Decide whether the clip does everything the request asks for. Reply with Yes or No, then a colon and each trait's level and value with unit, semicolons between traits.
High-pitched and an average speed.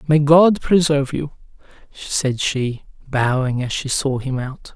No: medium, 140 Hz; average, 150 wpm